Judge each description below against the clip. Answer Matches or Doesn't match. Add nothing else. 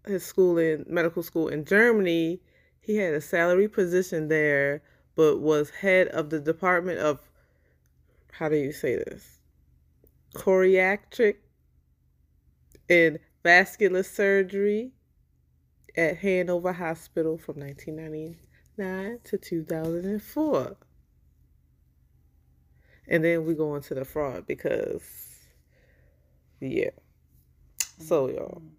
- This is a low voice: Doesn't match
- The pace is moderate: Doesn't match